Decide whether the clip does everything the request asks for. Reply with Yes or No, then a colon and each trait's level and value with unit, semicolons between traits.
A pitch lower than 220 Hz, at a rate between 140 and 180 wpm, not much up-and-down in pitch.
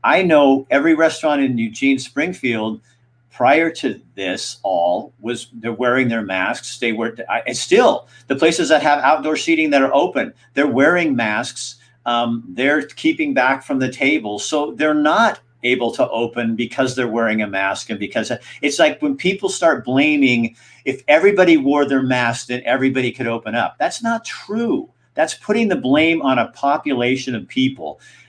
No: low, 135 Hz; average, 170 wpm; average, 4.3 semitones